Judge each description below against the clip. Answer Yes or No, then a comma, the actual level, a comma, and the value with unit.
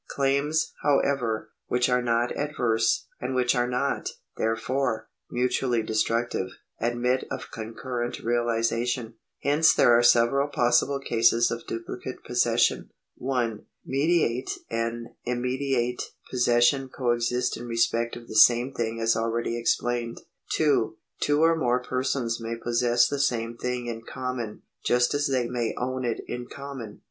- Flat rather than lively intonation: Yes, narrow, 1.9 semitones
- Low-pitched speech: Yes, low, 120 Hz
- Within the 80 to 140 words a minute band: Yes, slow, 135 wpm